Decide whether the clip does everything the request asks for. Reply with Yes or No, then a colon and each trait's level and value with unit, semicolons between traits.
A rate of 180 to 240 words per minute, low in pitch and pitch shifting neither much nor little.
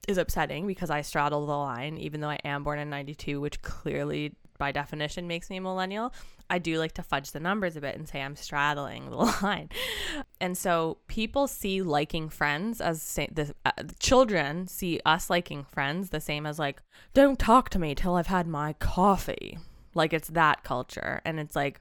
No: average, 195 wpm; medium, 160 Hz; average, 4.1 semitones